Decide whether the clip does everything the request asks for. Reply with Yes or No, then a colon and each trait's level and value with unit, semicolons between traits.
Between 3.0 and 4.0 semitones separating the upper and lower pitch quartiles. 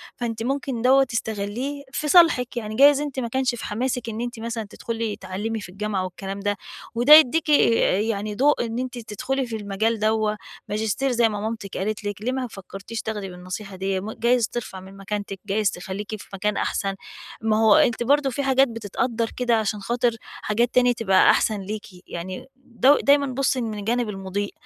Yes: average, 3.4 semitones